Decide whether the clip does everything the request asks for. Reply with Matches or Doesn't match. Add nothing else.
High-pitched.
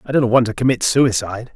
Doesn't match